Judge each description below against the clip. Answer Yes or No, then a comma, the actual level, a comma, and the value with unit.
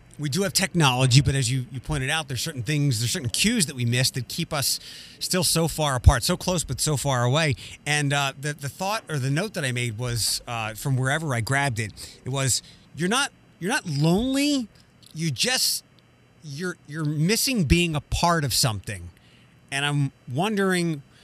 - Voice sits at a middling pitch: Yes, medium, 145 Hz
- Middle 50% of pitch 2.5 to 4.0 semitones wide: No, average, 4.5 semitones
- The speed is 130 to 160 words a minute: No, average, 200 wpm